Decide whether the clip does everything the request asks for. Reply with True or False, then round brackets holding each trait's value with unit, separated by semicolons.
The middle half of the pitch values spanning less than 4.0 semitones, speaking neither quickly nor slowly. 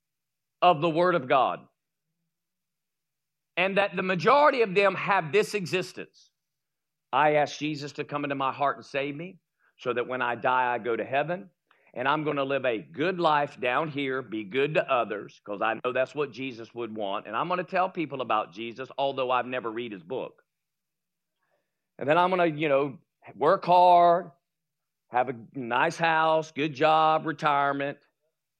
False (4.4 semitones; 180 wpm)